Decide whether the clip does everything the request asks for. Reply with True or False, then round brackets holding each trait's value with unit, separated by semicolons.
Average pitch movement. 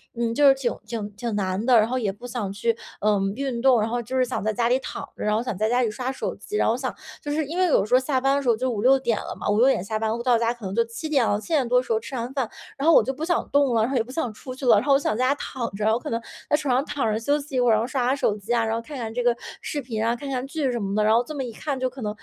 True (3.3 semitones)